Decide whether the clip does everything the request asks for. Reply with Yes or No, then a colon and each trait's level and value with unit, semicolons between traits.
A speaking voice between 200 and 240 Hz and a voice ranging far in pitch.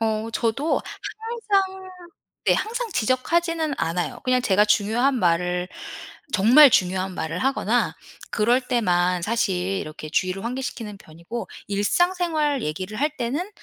Yes: high, 230 Hz; wide, 7.9 semitones